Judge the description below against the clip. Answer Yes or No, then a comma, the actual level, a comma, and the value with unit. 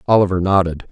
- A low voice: Yes, very low, 95 Hz